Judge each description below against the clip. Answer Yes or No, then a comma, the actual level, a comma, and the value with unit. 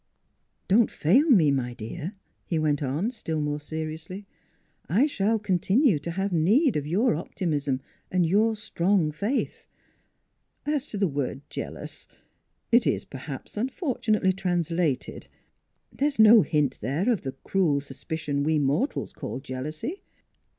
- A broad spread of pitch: Yes, wide, 6.4 semitones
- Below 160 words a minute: Yes, average, 140 wpm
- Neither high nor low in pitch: Yes, medium, 170 Hz